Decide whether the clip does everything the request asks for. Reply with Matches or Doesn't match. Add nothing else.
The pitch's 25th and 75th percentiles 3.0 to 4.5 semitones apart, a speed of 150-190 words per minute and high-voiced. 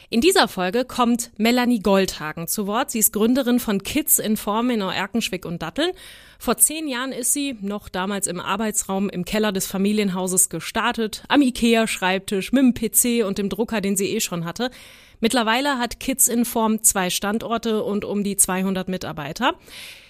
Matches